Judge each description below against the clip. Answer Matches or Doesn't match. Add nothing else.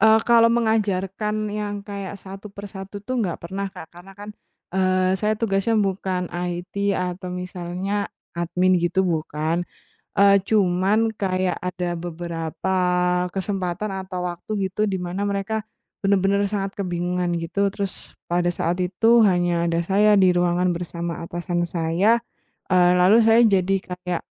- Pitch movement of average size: Doesn't match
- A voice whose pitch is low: Doesn't match